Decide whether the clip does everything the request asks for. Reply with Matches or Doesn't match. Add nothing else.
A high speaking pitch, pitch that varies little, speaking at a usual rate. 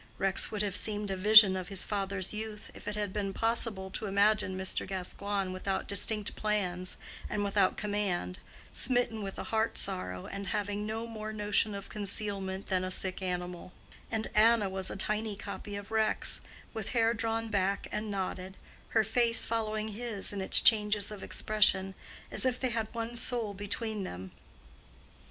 Matches